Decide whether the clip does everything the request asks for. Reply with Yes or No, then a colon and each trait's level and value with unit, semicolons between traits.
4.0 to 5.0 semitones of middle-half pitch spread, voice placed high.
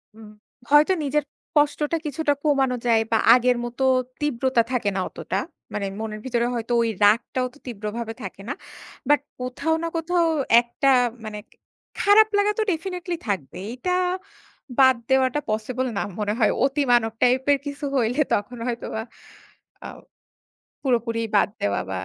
Yes: average, 4.5 semitones; very high, 250 Hz